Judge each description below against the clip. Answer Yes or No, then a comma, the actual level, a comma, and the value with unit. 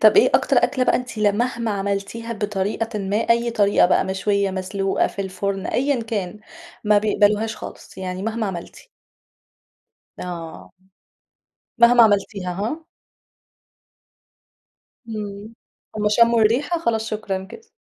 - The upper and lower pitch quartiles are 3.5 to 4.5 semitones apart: No, average, 2.8 semitones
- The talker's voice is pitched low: No, high, 210 Hz